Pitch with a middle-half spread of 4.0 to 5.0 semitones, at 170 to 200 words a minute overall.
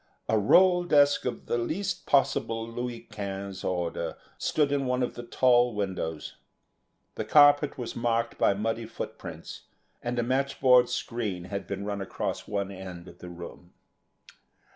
No: average, 4.6 semitones; average, 150 wpm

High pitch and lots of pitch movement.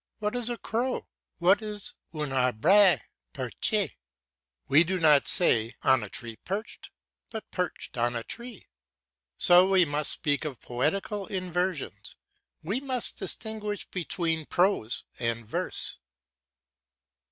No: medium, 180 Hz; wide, 7.3 semitones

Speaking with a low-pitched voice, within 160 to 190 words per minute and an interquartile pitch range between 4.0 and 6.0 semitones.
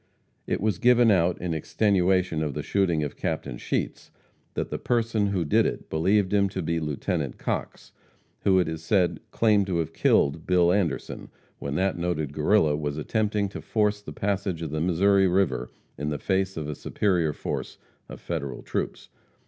Yes: very low, 90 Hz; average, 180 wpm; average, 4.3 semitones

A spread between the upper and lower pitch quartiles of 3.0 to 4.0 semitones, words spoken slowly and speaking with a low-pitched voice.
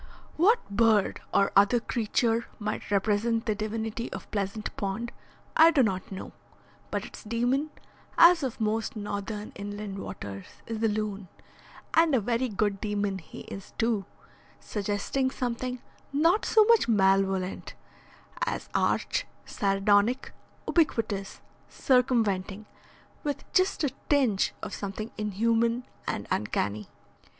No: average, 3.7 semitones; slow, 125 wpm; high, 215 Hz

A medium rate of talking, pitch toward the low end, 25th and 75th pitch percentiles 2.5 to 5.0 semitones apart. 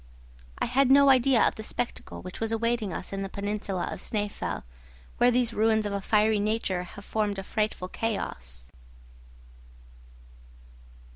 No: average, 150 wpm; high, 215 Hz; average, 2.8 semitones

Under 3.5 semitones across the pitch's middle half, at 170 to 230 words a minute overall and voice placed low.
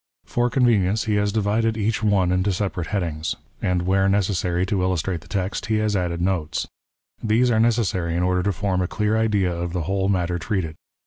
Yes: average, 3.1 semitones; fast, 205 wpm; very low, 95 Hz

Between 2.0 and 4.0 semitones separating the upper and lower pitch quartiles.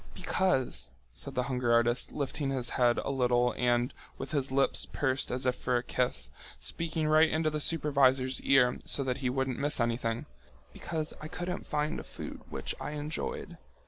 Yes: average, 3.4 semitones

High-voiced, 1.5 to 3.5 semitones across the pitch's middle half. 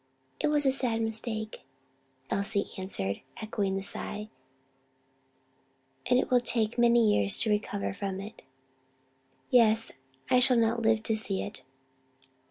Yes: high, 220 Hz; average, 2.7 semitones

